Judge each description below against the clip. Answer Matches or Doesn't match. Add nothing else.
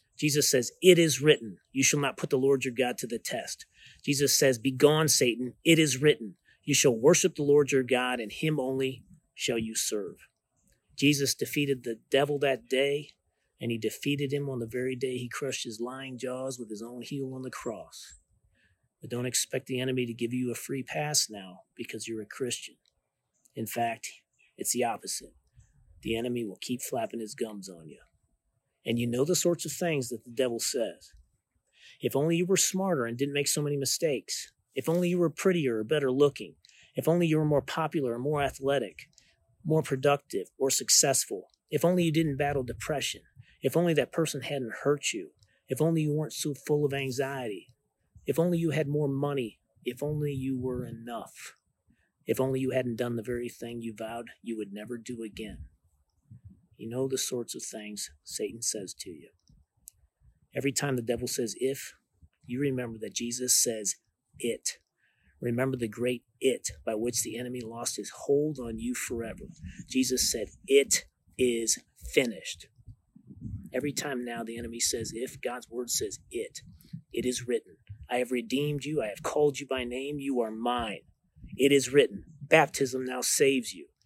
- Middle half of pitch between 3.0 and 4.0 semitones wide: Matches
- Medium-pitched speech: Doesn't match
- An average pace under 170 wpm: Doesn't match